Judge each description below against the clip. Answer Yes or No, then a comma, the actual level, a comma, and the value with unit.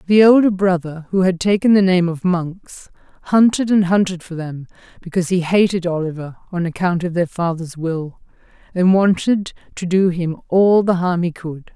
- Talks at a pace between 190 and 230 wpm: No, average, 180 wpm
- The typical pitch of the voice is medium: Yes, medium, 180 Hz